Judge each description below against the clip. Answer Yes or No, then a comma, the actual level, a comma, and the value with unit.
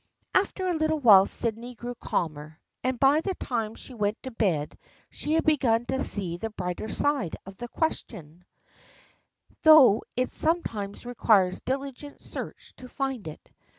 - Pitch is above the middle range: Yes, high, 240 Hz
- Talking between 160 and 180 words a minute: No, average, 150 wpm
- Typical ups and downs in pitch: No, wide, 5.7 semitones